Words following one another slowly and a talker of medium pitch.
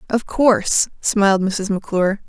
No: slow, 130 wpm; high, 205 Hz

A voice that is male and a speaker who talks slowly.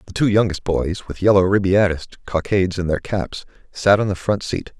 No: male; average, 200 wpm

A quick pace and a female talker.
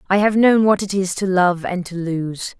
Yes: fast, 255 wpm; female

